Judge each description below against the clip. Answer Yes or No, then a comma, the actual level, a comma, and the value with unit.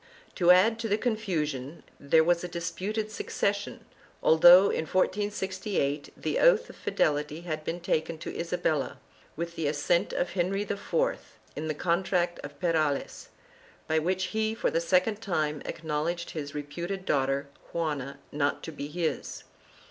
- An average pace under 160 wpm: Yes, average, 150 wpm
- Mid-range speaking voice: Yes, medium, 170 Hz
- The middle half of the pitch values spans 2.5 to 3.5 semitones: No, average, 4.0 semitones